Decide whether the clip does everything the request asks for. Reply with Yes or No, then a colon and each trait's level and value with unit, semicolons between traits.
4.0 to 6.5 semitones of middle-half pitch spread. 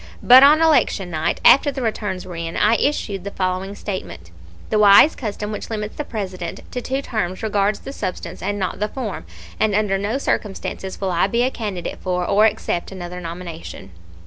No: average, 3.3 semitones